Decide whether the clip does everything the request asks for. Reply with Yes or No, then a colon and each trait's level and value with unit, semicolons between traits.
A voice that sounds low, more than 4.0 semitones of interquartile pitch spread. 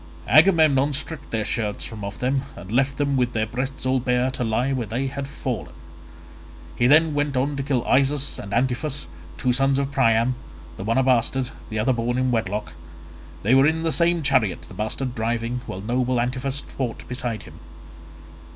No: low, 130 Hz; average, 3.0 semitones